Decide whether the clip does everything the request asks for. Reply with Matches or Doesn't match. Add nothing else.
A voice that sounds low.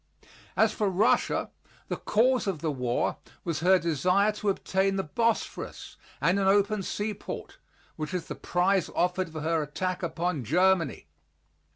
Doesn't match